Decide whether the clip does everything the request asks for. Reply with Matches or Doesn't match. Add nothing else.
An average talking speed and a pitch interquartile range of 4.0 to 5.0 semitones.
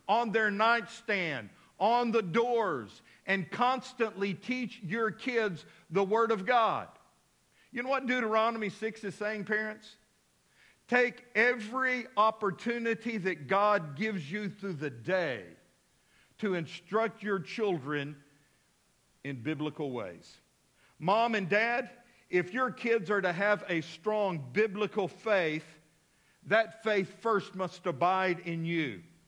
Doesn't match